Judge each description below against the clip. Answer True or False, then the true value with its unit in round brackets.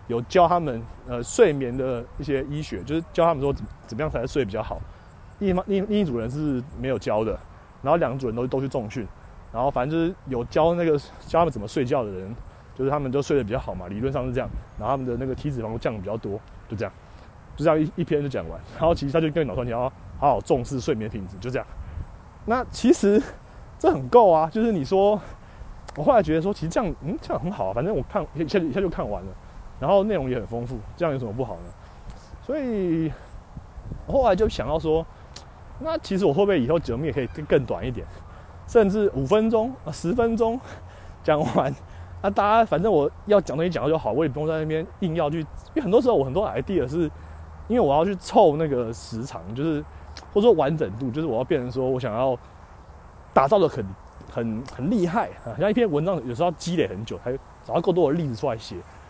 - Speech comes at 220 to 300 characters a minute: False (330 characters per minute)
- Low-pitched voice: True (130 Hz)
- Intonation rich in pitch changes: True (7.9 semitones)